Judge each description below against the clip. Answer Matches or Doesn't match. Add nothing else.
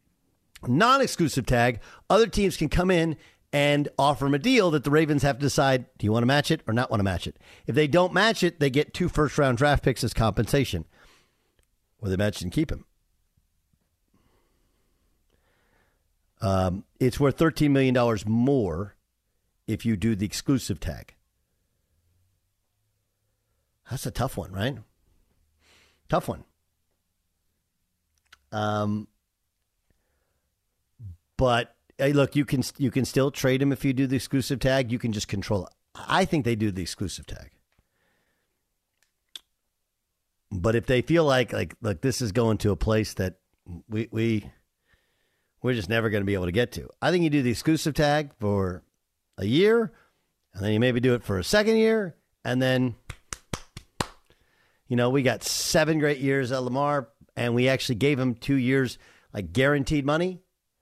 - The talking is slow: Doesn't match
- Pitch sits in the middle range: Doesn't match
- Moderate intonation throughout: Doesn't match